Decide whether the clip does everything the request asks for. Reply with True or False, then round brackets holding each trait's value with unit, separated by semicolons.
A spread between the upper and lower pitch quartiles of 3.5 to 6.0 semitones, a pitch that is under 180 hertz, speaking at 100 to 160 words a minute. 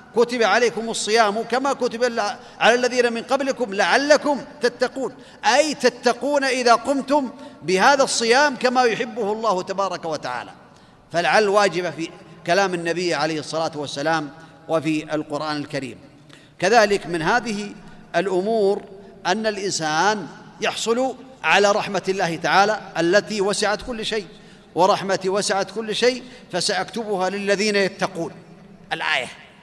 False (5.2 semitones; 205 Hz; 115 wpm)